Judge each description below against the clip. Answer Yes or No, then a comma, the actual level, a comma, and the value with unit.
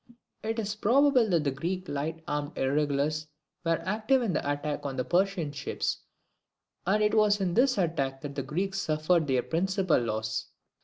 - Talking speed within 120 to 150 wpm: No, average, 170 wpm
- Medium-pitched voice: Yes, medium, 165 Hz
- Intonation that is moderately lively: No, wide, 5.7 semitones